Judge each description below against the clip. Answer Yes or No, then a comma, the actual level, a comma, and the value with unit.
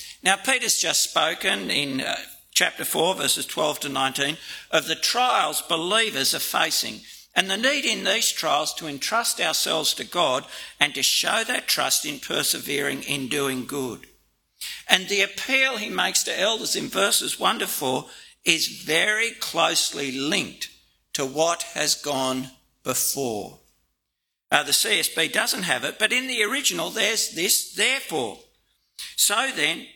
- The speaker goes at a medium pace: Yes, average, 150 wpm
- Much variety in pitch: Yes, wide, 7.5 semitones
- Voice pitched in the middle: Yes, medium, 170 Hz